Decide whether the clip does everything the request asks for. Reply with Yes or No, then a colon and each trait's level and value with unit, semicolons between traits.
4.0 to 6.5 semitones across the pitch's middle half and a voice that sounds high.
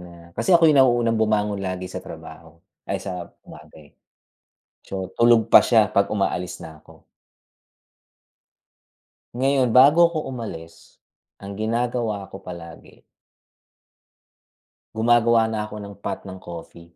No: average, 4.6 semitones; low, 105 Hz